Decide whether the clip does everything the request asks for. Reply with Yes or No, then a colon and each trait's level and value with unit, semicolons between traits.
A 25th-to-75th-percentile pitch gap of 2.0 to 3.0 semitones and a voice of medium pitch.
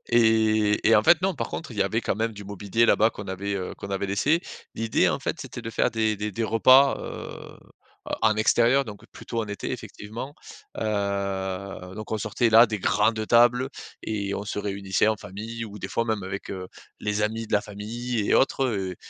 No: narrow, 2.4 semitones; low, 110 Hz